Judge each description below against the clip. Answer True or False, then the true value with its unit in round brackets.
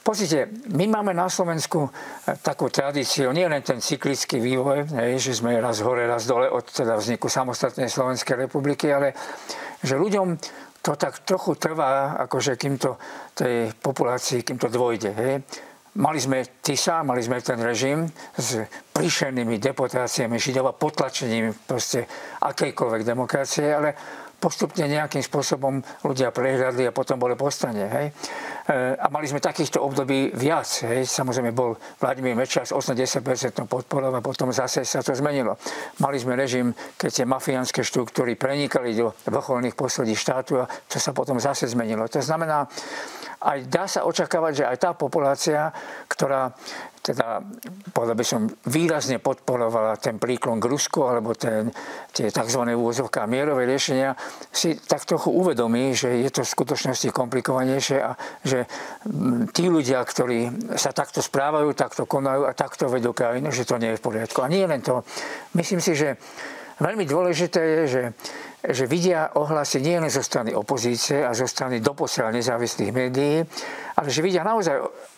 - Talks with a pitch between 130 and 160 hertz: True (135 Hz)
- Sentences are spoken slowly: False (150 wpm)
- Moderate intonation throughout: True (3.4 semitones)